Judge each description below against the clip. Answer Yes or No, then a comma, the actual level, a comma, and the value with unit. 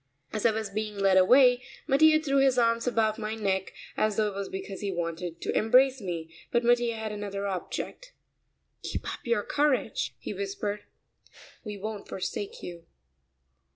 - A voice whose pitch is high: Yes, high, 215 Hz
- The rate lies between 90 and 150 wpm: No, average, 165 wpm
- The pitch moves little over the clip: No, average, 3.8 semitones